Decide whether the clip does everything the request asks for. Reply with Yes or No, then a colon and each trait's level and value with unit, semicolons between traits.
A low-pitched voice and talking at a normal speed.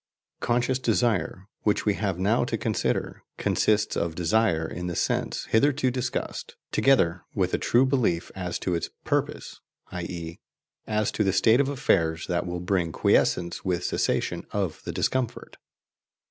Yes: very low, 95 Hz; average, 150 wpm